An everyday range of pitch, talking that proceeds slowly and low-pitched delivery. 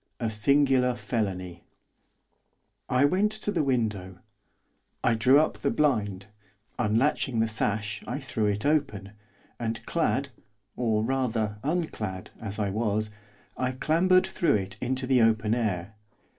Yes: average, 4.5 semitones; slow, 130 wpm; low, 115 Hz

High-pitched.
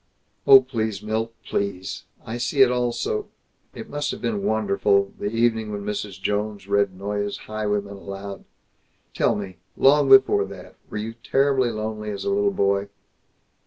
No: low, 110 Hz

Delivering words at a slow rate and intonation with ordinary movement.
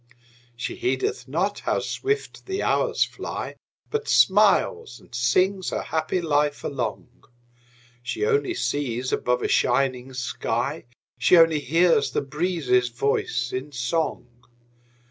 No: slow, 125 wpm; wide, 6.3 semitones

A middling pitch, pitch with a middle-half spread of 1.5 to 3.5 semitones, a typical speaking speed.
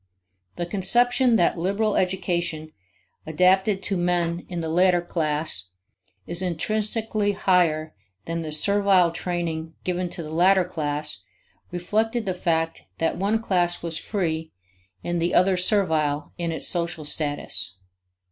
No: medium, 175 Hz; average, 2.9 semitones; slow, 130 wpm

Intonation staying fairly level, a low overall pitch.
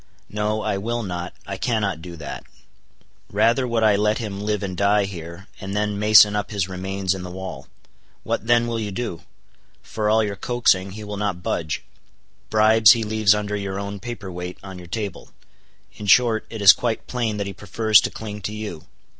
Yes: narrow, 2.3 semitones; low, 105 Hz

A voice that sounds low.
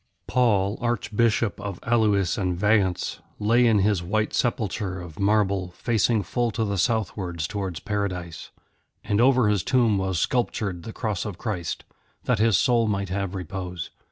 Yes: low, 100 Hz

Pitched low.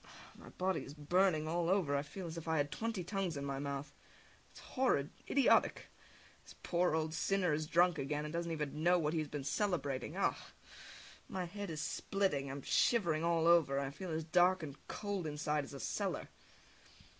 No: medium, 160 Hz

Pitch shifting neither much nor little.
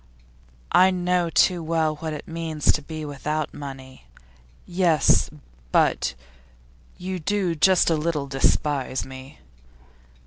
Yes: average, 3.2 semitones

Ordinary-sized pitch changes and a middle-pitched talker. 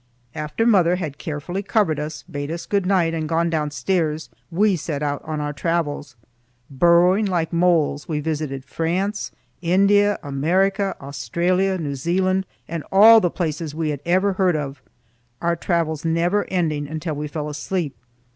Yes: average, 3.7 semitones; medium, 165 Hz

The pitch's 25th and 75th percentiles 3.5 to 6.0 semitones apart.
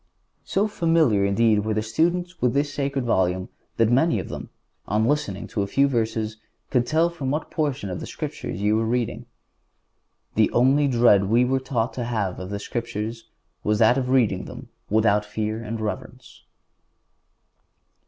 Yes: average, 4.1 semitones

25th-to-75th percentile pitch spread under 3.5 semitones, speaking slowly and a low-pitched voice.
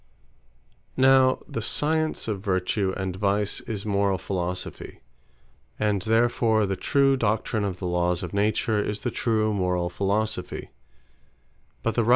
Yes: average, 3.0 semitones; slow, 125 wpm; low, 105 Hz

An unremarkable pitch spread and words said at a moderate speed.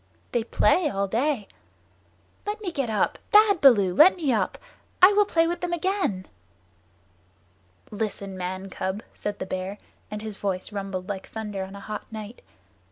No: wide, 8.8 semitones; average, 165 wpm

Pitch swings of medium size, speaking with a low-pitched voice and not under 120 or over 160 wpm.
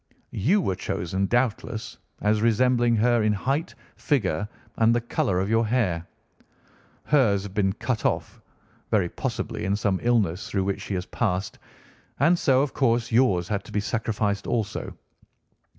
Yes: average, 3.7 semitones; low, 110 Hz; average, 155 wpm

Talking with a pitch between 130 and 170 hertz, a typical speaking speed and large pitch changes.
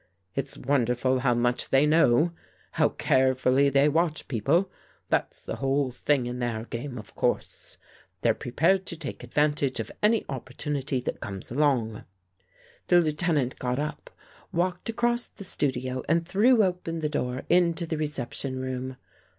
No: medium, 140 Hz; average, 150 wpm; average, 4.6 semitones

